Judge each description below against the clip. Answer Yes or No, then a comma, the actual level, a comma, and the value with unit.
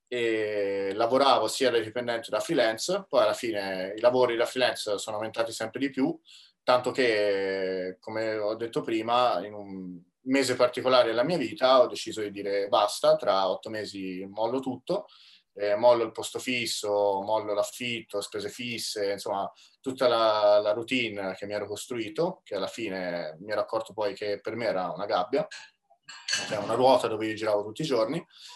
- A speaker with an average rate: No, fast, 175 wpm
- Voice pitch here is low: Yes, low, 110 Hz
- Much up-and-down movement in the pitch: No, average, 3.2 semitones